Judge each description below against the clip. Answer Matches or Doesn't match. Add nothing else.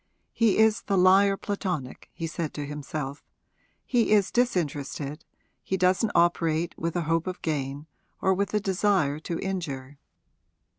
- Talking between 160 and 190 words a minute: Doesn't match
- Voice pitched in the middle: Matches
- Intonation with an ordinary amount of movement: Matches